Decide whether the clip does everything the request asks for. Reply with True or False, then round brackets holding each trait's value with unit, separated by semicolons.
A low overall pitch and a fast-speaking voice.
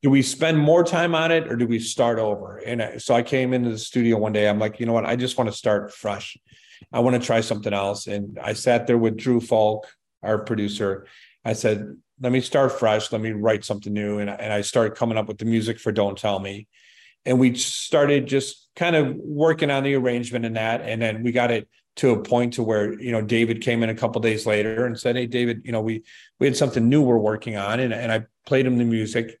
True (115 Hz; 250 wpm)